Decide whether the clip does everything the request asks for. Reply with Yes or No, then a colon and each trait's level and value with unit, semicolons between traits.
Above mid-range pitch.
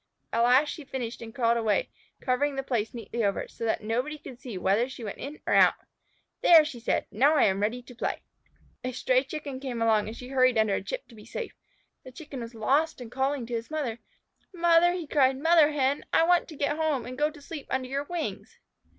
Yes: very high, 260 Hz